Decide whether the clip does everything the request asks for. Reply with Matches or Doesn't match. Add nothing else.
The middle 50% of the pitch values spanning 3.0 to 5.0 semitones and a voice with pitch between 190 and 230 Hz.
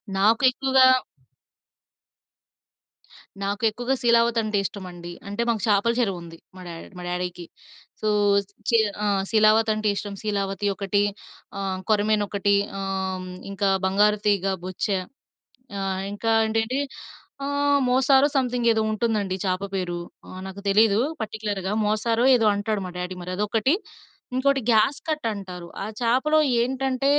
Matches